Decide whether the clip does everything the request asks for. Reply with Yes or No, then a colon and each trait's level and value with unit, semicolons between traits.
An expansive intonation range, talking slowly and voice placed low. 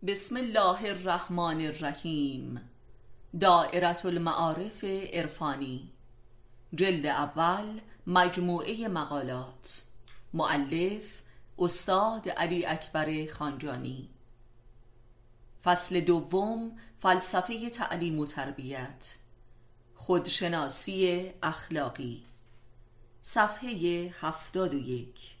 No: wide, 6.8 semitones; slow, 65 wpm; medium, 160 Hz